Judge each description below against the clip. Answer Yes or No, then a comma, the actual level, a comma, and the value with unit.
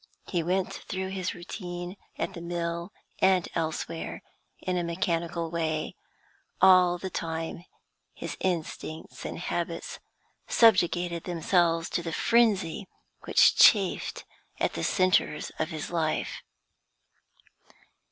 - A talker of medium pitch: Yes, medium, 175 Hz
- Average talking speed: No, slow, 115 wpm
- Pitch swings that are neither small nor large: No, narrow, 1.9 semitones